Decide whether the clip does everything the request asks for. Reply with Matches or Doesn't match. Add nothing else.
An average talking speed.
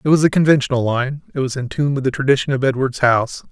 Doesn't match